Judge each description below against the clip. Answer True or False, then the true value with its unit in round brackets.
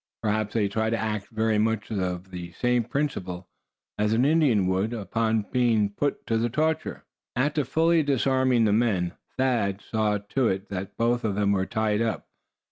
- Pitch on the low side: True (110 Hz)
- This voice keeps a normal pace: True (175 wpm)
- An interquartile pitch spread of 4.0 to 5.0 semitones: False (3.3 semitones)